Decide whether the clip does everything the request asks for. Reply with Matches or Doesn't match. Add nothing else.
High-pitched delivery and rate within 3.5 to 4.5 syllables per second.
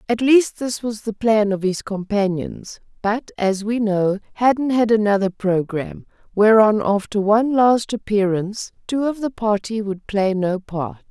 Matches